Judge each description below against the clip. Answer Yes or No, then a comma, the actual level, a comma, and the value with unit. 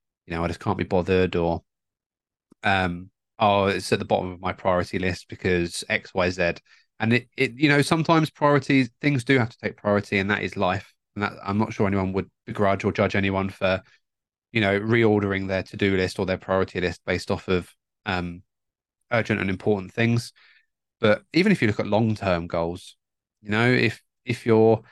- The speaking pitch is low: Yes, low, 100 Hz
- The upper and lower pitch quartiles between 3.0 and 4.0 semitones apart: Yes, average, 3.7 semitones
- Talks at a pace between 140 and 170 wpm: No, average, 195 wpm